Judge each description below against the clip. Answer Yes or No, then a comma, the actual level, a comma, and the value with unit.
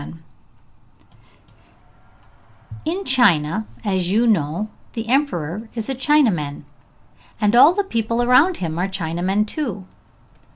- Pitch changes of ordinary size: No, wide, 6.3 semitones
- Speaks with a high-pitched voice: Yes, high, 215 Hz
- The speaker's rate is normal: No, slow, 115 wpm